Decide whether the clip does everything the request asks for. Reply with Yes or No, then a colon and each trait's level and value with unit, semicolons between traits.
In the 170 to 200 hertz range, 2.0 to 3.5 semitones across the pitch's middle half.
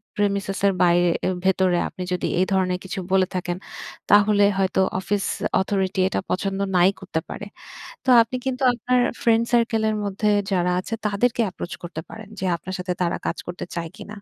Yes: high, 190 Hz; narrow, 2.6 semitones